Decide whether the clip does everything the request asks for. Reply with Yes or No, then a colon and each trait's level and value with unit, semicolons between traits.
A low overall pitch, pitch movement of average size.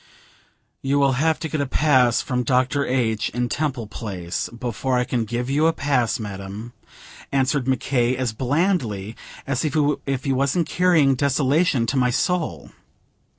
Yes: low, 130 Hz; average, 3.2 semitones